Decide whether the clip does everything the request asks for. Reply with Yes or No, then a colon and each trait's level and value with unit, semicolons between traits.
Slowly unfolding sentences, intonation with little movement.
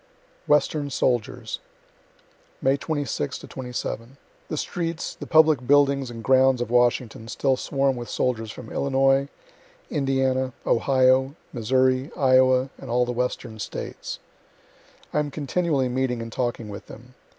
Yes: slow, 130 wpm; narrow, 2.1 semitones